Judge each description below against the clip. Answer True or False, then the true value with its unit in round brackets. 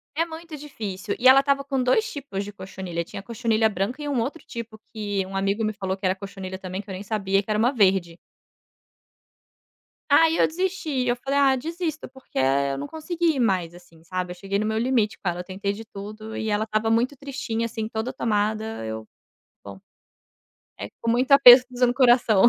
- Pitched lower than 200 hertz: False (220 Hz)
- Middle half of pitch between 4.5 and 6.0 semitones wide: True (5.2 semitones)